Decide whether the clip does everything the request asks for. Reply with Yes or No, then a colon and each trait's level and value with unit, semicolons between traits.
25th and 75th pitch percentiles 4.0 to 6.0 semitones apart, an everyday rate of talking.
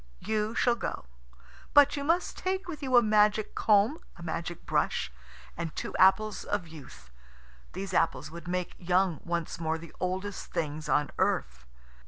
Yes: average, 4.6 semitones; average, 160 wpm